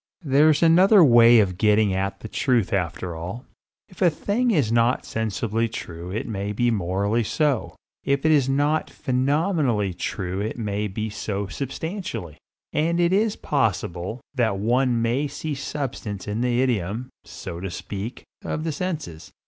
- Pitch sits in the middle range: No, low, 115 Hz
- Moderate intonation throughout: No, wide, 6.3 semitones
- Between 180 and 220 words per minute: No, average, 155 wpm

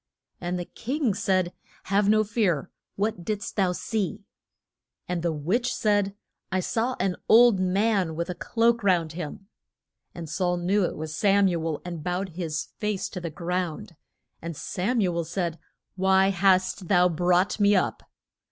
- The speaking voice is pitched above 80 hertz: Yes, medium, 185 Hz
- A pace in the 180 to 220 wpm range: No, average, 165 wpm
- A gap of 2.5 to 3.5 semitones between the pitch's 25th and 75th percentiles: Yes, average, 2.9 semitones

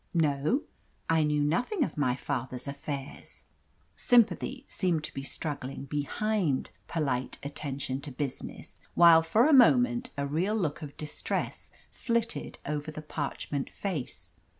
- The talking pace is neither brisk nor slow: No, slow, 130 wpm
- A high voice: No, medium, 150 Hz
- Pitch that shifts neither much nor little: No, wide, 7.2 semitones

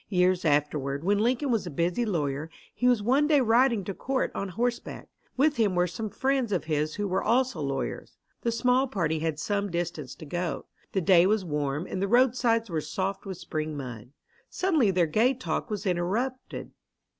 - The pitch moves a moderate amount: No, wide, 6.9 semitones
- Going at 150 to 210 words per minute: Yes, average, 190 wpm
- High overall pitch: Yes, high, 195 Hz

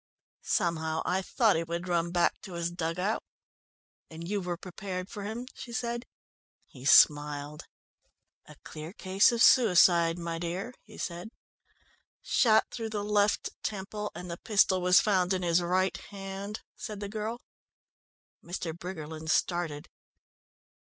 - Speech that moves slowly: No, average, 145 wpm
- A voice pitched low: No, medium, 180 Hz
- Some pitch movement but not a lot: Yes, average, 3.5 semitones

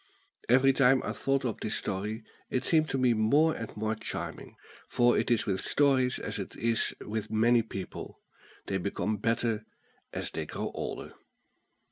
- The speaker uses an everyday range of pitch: Yes, average, 3.2 semitones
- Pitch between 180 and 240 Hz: No, low, 115 Hz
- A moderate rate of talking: Yes, average, 165 wpm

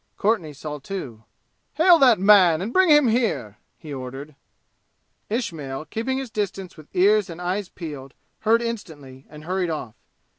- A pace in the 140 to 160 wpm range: Yes, average, 150 wpm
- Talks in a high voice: No, medium, 180 Hz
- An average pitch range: No, wide, 7.0 semitones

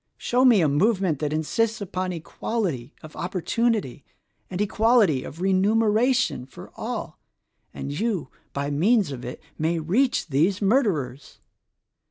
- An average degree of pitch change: No, wide, 6.8 semitones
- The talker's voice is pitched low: No, medium, 185 Hz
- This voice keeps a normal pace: No, slow, 130 wpm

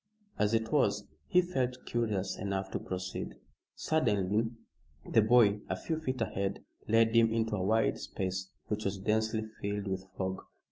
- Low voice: Yes, low, 110 Hz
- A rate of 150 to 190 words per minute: Yes, average, 155 wpm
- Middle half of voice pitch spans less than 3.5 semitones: Yes, average, 2.8 semitones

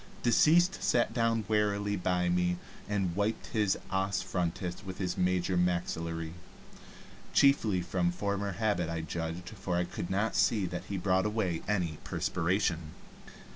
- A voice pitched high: No, very low, 90 Hz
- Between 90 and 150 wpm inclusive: Yes, average, 140 wpm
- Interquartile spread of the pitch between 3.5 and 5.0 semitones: No, average, 2.7 semitones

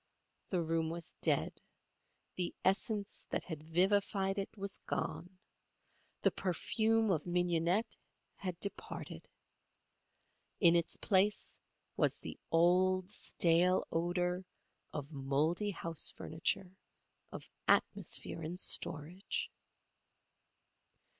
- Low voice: No, medium, 180 Hz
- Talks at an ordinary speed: No, slow, 95 wpm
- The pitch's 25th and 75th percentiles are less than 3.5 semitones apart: Yes, average, 2.8 semitones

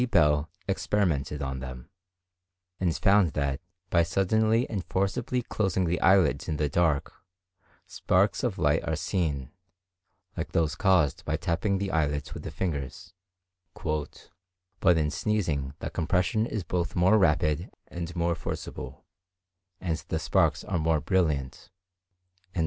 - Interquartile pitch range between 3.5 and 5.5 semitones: Yes, average, 4.1 semitones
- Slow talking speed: Yes, slow, 130 wpm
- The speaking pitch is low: Yes, very low, 85 Hz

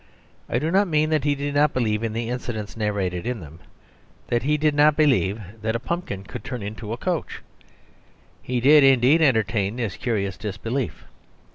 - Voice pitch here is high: No, low, 120 Hz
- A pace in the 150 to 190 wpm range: Yes, average, 180 wpm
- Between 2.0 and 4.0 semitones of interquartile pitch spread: No, wide, 5.4 semitones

